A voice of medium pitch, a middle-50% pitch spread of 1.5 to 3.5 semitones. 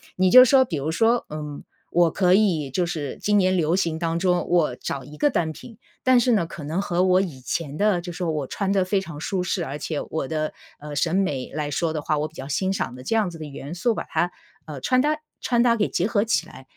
No: medium, 170 Hz; average, 4.4 semitones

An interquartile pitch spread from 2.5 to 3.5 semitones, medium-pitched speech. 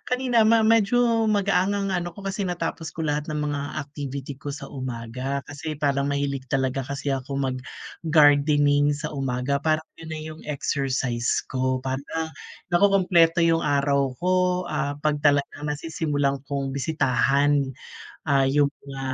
Yes: average, 3.0 semitones; medium, 145 Hz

